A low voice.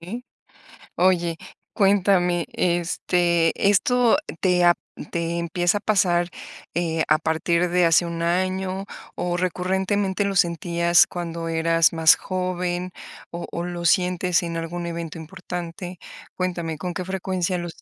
No: medium, 175 Hz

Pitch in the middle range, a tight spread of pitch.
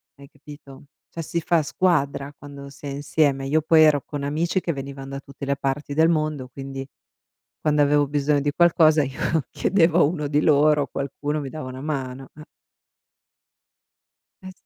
Yes: medium, 145 Hz; narrow, 2.0 semitones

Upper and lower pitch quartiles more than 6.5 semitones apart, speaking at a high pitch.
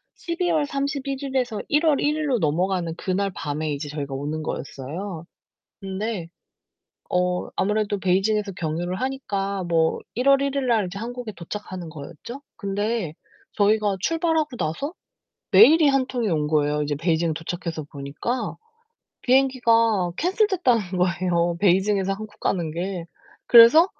Yes: wide, 6.9 semitones; high, 195 Hz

